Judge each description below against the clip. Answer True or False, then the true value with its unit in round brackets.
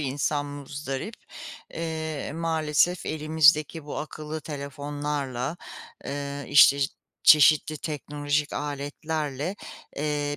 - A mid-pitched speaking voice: True (150 Hz)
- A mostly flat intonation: True (1.5 semitones)